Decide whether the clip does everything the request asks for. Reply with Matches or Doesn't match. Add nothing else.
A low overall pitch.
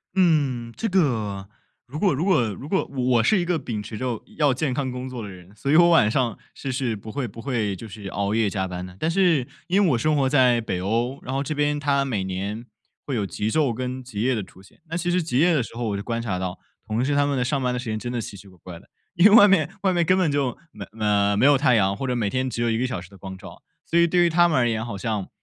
Matches